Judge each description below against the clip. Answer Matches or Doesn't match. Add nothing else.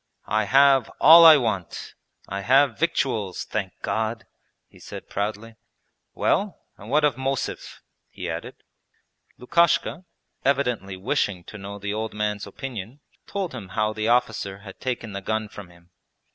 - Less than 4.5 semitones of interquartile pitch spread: Doesn't match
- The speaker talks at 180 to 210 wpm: Doesn't match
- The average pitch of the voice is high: Doesn't match